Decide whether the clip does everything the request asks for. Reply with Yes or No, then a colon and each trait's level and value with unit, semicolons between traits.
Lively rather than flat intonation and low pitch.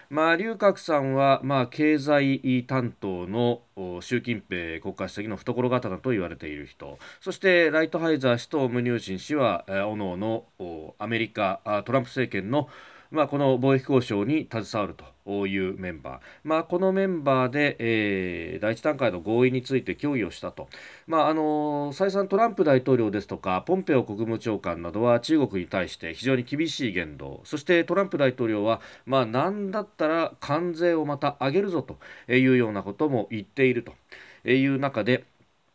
Yes: wide, 6.4 semitones; low, 125 Hz